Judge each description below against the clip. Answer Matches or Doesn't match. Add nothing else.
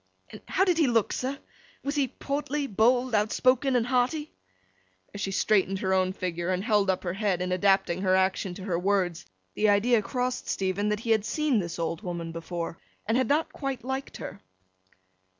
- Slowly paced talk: Doesn't match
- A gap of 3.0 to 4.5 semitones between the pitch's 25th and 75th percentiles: Doesn't match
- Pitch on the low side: Doesn't match